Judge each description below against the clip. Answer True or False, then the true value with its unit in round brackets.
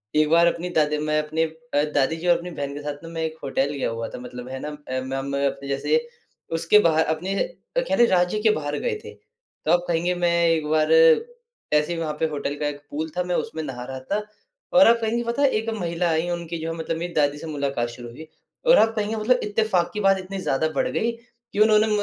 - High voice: False (165 Hz)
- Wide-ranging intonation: False (4.7 semitones)